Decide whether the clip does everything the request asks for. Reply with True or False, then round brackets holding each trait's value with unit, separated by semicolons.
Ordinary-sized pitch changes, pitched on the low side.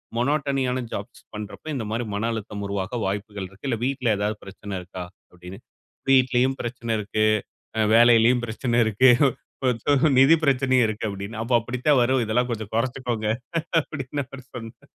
True (3.4 semitones; 120 Hz)